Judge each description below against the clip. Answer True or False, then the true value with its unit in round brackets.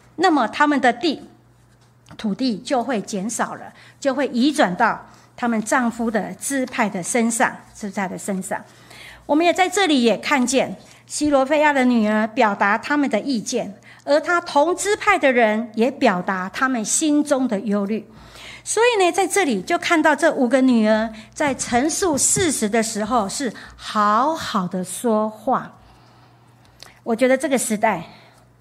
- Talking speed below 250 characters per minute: True (225 characters per minute)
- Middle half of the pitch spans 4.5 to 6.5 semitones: True (5.5 semitones)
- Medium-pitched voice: False (240 Hz)